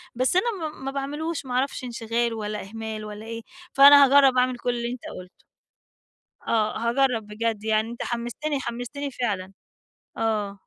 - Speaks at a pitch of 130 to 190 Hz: No, high, 235 Hz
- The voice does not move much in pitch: No, average, 3.6 semitones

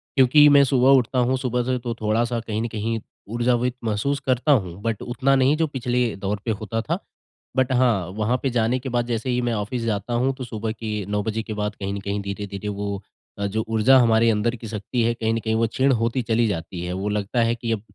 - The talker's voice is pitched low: Yes, low, 115 Hz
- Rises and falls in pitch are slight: No, average, 3.0 semitones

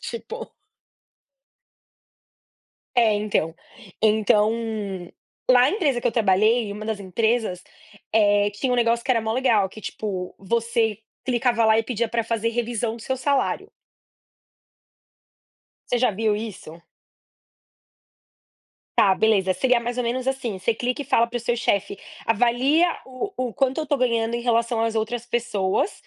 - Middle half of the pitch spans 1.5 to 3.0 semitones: Yes, narrow, 2.5 semitones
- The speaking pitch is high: Yes, high, 230 Hz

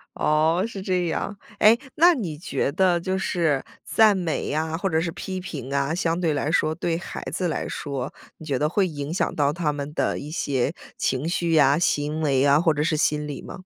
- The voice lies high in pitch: No, medium, 160 Hz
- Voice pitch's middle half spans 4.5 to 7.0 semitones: No, average, 3.4 semitones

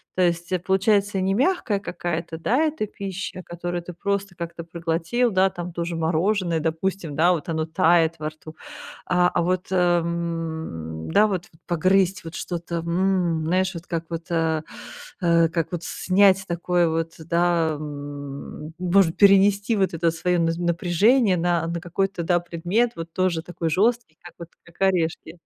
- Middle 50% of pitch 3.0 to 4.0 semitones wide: No, narrow, 2.4 semitones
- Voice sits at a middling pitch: Yes, medium, 175 Hz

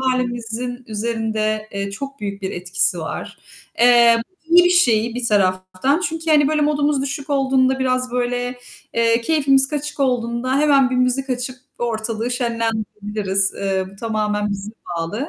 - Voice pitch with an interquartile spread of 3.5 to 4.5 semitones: Yes, average, 3.9 semitones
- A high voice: Yes, high, 240 Hz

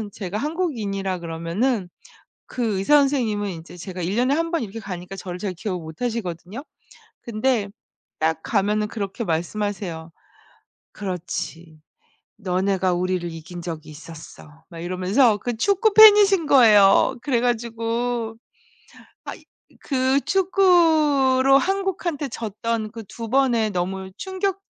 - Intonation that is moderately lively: No, wide, 6.5 semitones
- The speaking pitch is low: No, high, 215 Hz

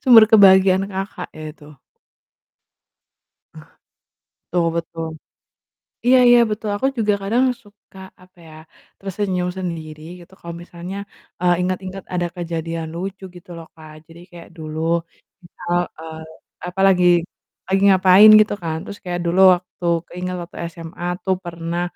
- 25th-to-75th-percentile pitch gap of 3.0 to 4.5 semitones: No, narrow, 2.5 semitones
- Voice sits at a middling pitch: Yes, medium, 180 Hz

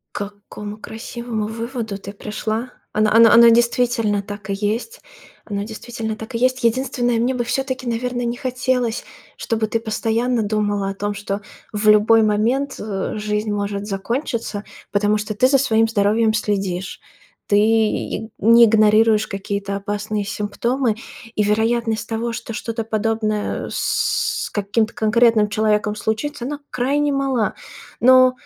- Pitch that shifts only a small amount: Yes, narrow, 2.3 semitones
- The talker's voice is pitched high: Yes, high, 220 Hz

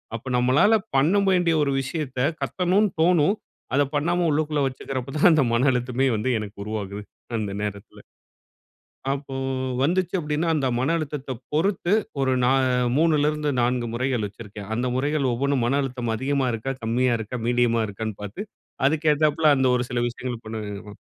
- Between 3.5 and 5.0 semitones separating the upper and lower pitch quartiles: Yes, average, 4.2 semitones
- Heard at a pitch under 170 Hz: Yes, low, 135 Hz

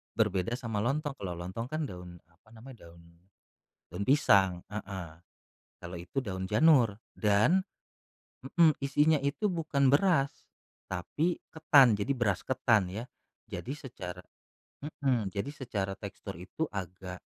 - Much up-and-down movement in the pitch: Yes, wide, 6.8 semitones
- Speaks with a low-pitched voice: Yes, low, 115 Hz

